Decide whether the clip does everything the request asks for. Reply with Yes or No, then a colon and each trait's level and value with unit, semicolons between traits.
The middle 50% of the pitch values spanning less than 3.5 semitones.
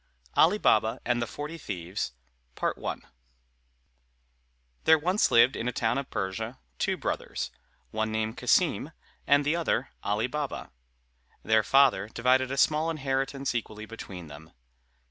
No: average, 4.4 semitones